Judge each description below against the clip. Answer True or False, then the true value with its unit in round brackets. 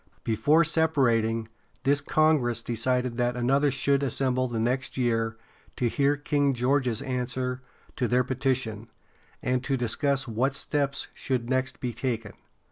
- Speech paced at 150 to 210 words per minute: False (135 wpm)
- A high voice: False (130 Hz)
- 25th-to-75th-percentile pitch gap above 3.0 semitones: False (2.5 semitones)